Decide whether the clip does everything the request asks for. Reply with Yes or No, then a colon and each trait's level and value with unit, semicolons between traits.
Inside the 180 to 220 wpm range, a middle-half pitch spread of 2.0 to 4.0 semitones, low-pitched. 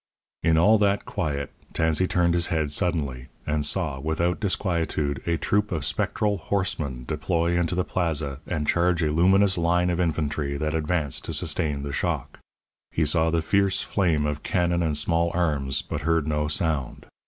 No: average, 170 wpm; average, 2.9 semitones; very low, 80 Hz